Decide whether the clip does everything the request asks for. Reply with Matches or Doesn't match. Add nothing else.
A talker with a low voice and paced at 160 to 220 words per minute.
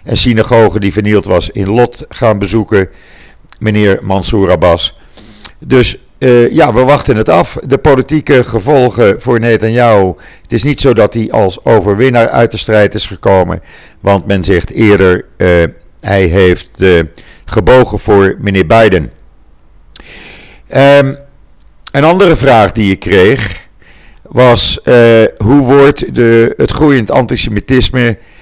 Doesn't match